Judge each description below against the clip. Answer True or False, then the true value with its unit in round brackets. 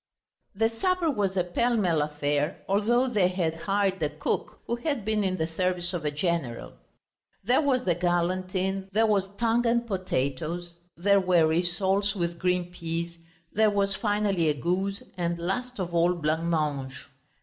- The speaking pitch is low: False (185 Hz)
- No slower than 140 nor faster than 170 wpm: True (160 wpm)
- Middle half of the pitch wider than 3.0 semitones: True (3.5 semitones)